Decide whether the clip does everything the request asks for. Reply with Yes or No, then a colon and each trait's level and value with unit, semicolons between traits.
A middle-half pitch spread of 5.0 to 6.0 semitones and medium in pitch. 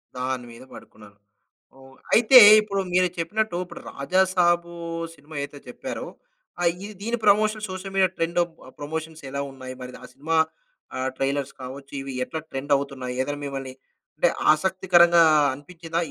Yes: wide, 5.5 semitones; medium, 160 Hz